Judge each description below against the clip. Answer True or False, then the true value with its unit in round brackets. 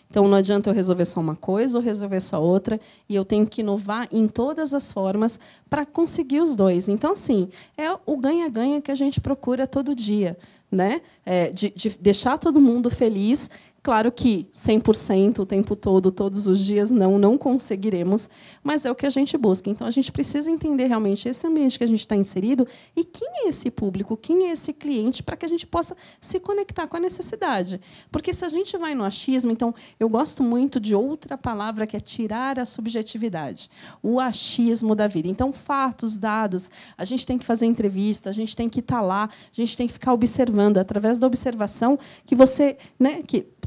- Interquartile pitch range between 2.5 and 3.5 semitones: False (5.2 semitones)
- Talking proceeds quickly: True (200 wpm)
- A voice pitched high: True (230 Hz)